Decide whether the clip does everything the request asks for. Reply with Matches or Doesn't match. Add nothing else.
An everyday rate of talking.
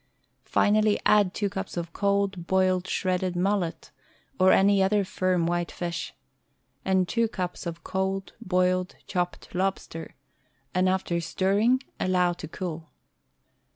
Doesn't match